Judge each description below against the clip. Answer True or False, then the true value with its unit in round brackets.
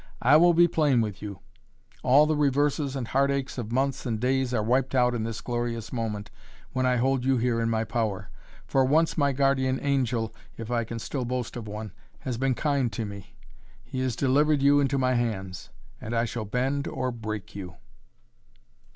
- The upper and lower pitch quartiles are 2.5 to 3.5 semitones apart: True (3.1 semitones)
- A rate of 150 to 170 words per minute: False (195 wpm)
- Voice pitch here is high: False (125 Hz)